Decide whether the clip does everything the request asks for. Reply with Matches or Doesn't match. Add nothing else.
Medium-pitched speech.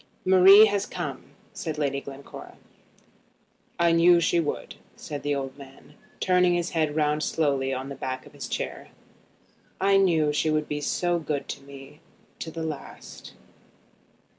Matches